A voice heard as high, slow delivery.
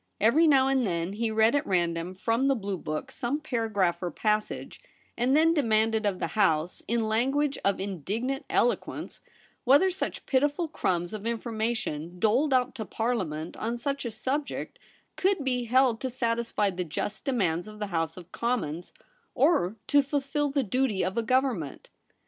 No: high, 230 Hz; average, 170 wpm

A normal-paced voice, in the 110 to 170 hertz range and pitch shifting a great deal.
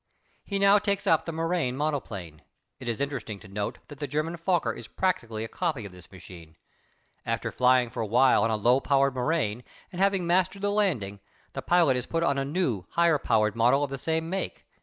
No: fast, 210 wpm; medium, 140 Hz; wide, 7.0 semitones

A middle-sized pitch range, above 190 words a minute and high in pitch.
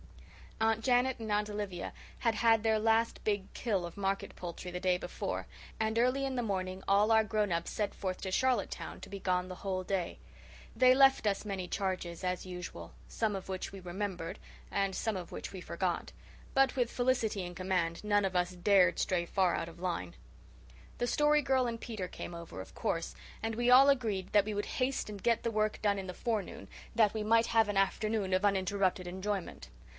Yes: average, 3.4 semitones; fast, 205 wpm; high, 200 Hz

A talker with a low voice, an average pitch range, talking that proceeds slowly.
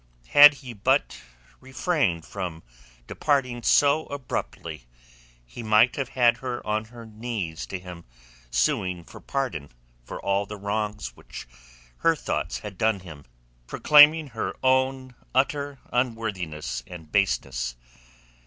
No: low, 110 Hz; wide, 6.6 semitones; slow, 125 wpm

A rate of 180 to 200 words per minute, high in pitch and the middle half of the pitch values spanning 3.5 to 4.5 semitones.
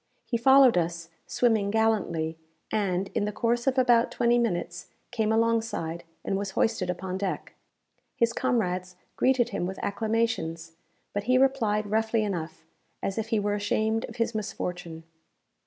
No: average, 150 wpm; high, 215 Hz; average, 4.0 semitones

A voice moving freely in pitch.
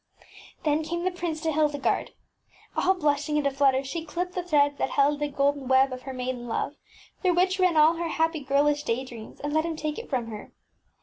No: average, 3.2 semitones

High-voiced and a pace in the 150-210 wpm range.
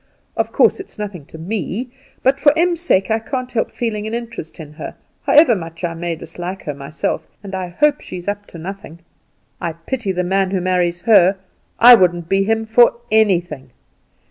Yes: high, 195 Hz; average, 190 wpm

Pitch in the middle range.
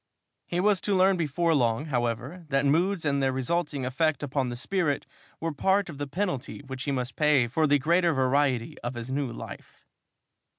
Yes: medium, 145 Hz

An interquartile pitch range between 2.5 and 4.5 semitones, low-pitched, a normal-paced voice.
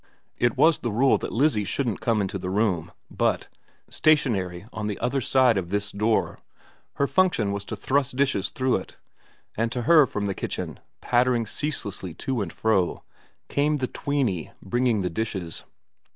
No: average, 4.9 semitones; low, 115 Hz; average, 165 wpm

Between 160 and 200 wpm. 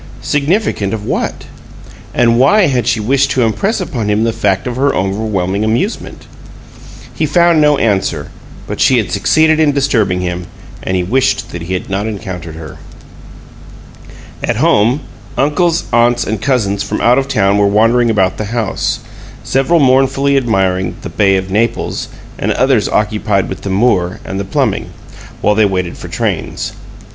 Yes: average, 165 wpm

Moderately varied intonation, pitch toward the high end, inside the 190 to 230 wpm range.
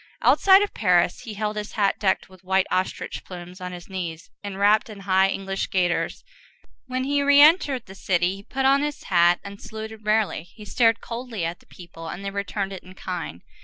Yes: average, 3.4 semitones; high, 195 Hz; average, 200 wpm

